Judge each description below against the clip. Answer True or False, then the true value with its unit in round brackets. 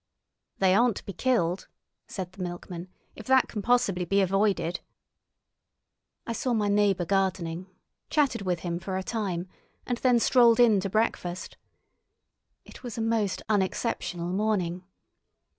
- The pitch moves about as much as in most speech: True (4.0 semitones)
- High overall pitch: True (195 Hz)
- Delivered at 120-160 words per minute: True (140 wpm)